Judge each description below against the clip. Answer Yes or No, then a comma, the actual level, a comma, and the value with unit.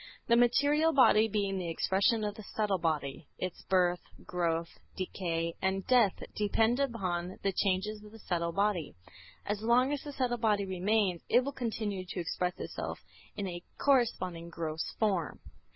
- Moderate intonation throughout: Yes, average, 4.2 semitones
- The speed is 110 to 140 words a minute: No, average, 160 wpm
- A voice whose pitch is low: No, high, 200 Hz